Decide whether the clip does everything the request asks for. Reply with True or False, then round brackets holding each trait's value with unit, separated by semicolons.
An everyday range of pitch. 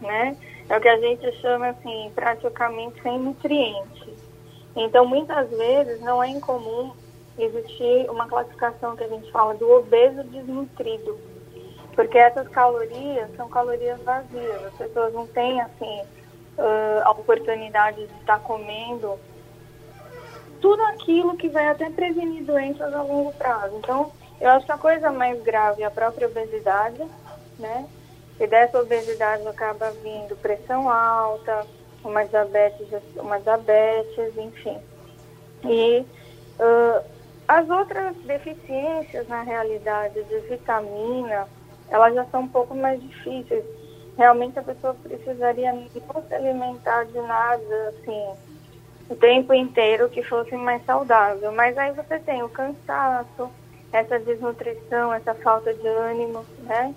True (3.2 semitones)